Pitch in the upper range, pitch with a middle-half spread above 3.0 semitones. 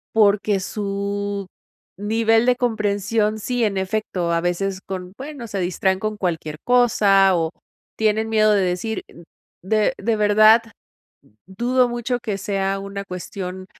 No: high, 205 Hz; narrow, 2.5 semitones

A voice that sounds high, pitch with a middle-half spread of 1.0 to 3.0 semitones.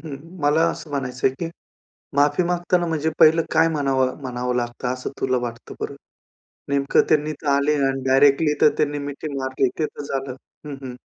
No: medium, 140 Hz; average, 2.7 semitones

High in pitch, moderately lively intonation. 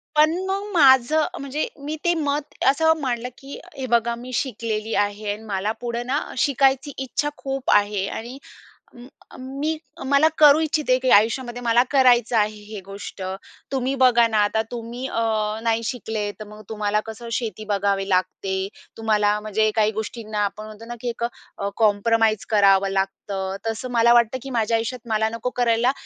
Yes: high, 230 Hz; average, 3.5 semitones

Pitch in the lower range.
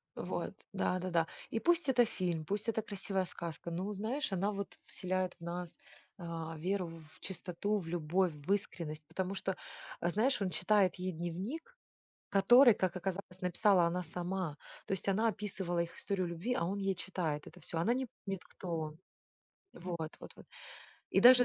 No: medium, 185 Hz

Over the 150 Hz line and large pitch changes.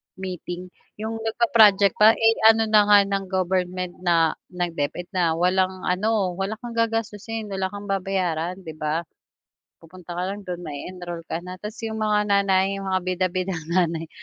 No: high, 190 Hz; average, 2.8 semitones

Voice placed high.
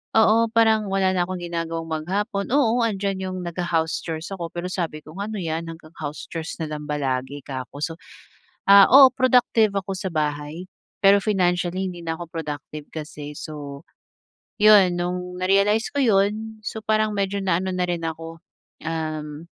No: medium, 180 Hz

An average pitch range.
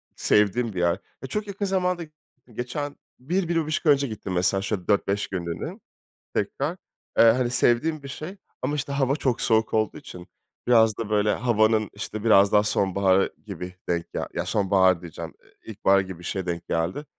No: wide, 6.2 semitones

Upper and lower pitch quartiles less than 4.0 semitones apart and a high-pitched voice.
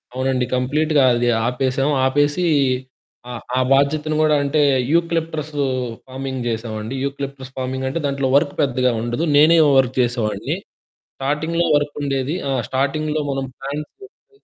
No: narrow, 2.6 semitones; medium, 140 Hz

